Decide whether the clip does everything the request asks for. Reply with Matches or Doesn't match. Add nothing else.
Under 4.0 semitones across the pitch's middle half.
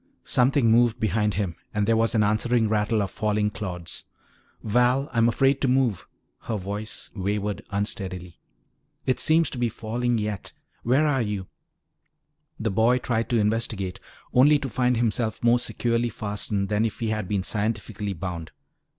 Matches